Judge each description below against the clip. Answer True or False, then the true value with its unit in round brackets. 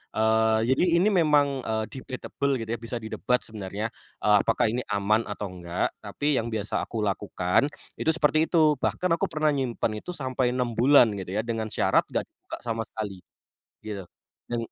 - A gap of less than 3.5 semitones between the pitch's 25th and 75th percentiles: False (3.8 semitones)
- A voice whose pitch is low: True (115 Hz)